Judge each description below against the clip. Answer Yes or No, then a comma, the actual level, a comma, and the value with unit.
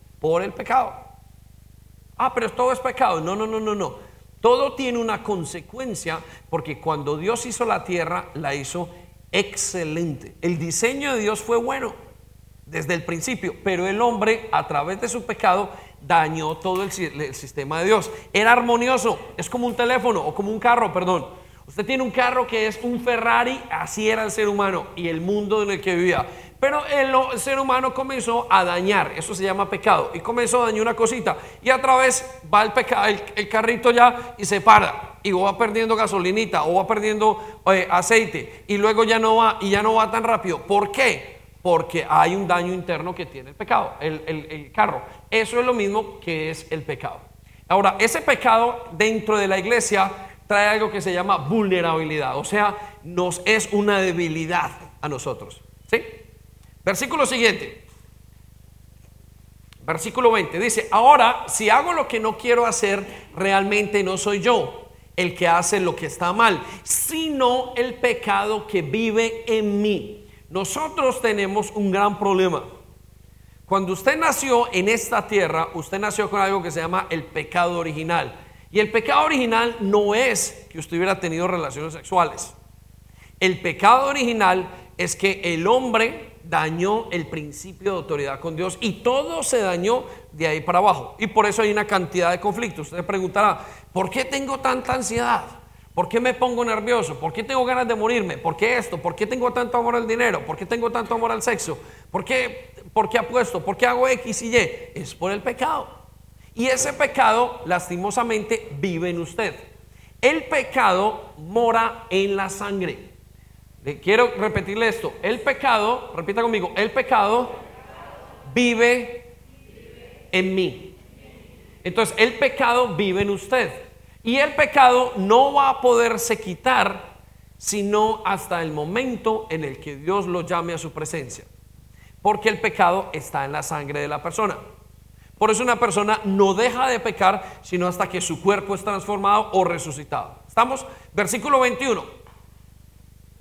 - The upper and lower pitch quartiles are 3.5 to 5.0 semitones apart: No, wide, 5.4 semitones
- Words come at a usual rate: Yes, average, 170 wpm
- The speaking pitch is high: Yes, high, 205 Hz